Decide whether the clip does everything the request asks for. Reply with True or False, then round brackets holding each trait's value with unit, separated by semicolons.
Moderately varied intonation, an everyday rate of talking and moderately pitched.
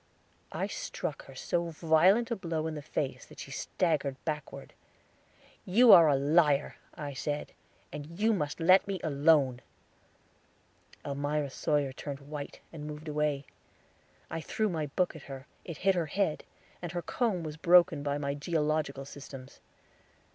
True (3.3 semitones; 155 wpm; 155 Hz)